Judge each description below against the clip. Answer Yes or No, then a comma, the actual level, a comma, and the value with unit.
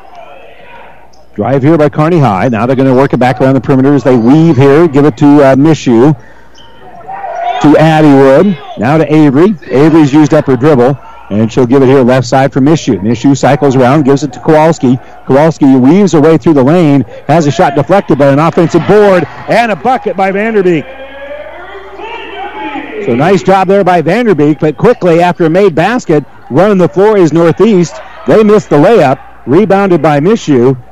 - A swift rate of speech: No, average, 180 wpm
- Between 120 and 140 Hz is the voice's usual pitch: No, medium, 155 Hz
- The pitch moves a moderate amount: No, wide, 5.7 semitones